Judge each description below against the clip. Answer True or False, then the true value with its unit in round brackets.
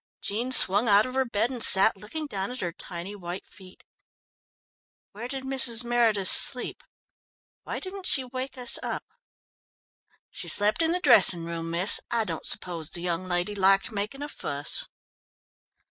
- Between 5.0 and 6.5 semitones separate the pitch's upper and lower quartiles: True (5.5 semitones)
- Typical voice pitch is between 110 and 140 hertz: False (210 Hz)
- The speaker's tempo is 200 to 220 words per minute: False (160 wpm)